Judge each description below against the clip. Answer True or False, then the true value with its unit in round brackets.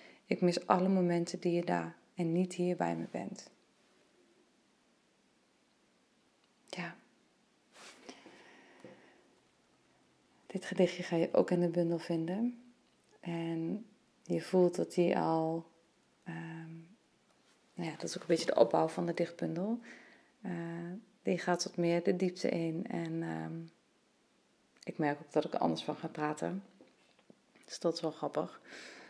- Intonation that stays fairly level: True (2.1 semitones)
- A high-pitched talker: False (170 Hz)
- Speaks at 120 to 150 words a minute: True (140 wpm)